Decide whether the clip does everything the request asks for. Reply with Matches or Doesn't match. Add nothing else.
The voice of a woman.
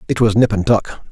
Doesn't match